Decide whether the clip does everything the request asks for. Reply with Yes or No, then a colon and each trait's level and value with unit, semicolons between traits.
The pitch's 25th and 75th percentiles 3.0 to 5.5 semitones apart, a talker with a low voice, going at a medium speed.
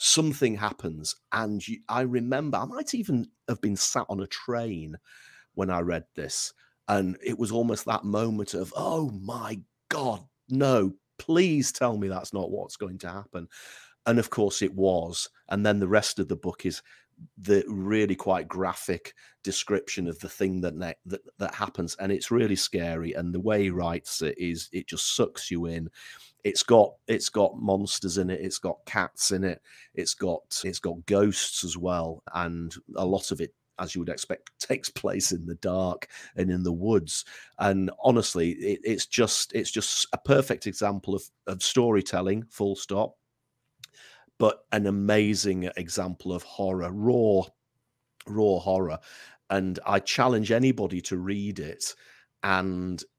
Yes: average, 3.5 semitones; low, 100 Hz; average, 170 wpm